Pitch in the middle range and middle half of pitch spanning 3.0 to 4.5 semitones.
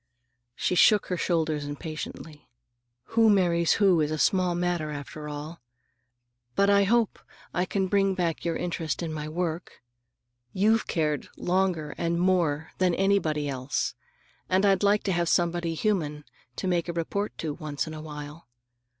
Yes: medium, 170 Hz; average, 3.6 semitones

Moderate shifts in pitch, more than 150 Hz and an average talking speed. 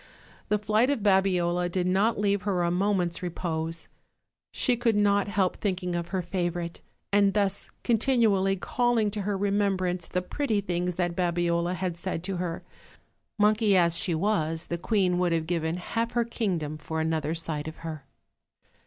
Yes: average, 3.1 semitones; medium, 185 Hz; average, 170 wpm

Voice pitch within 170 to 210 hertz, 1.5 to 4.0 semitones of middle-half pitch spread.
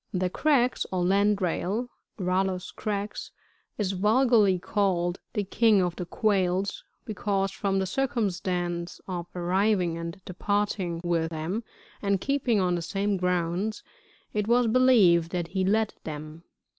Yes: high, 190 Hz; average, 3.0 semitones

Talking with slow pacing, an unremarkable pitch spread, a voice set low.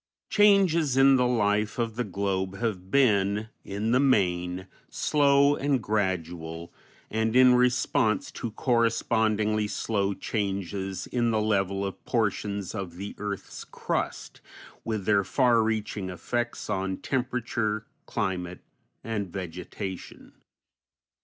Yes: slow, 115 wpm; average, 3.7 semitones; low, 105 Hz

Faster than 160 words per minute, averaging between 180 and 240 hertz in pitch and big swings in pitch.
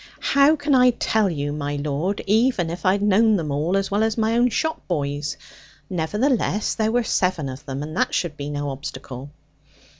Yes: average, 200 wpm; medium, 185 Hz; wide, 7.3 semitones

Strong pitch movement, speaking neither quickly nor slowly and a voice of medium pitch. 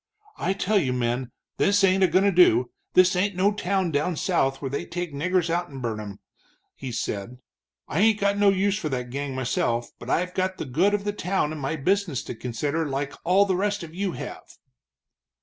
No: wide, 6.3 semitones; fast, 215 wpm; medium, 170 Hz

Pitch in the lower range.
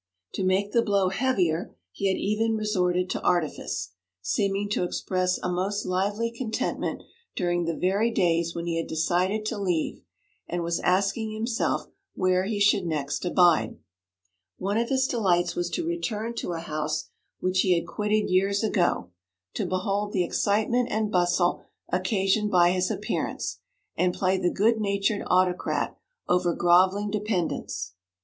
No: medium, 185 Hz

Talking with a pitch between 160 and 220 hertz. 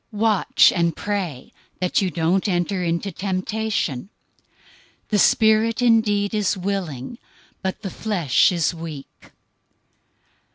Yes: high, 190 Hz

